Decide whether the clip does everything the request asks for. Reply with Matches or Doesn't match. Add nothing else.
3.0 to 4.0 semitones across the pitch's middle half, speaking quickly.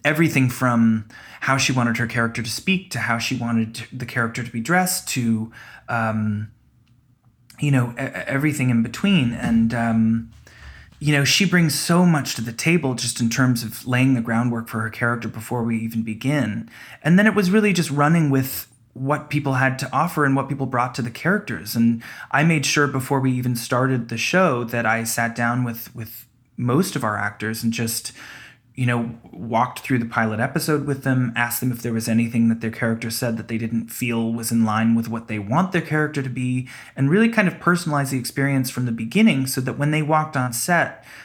Matches